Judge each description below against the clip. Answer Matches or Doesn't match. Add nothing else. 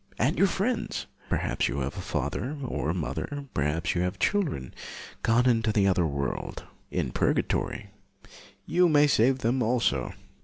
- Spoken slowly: Doesn't match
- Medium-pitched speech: Doesn't match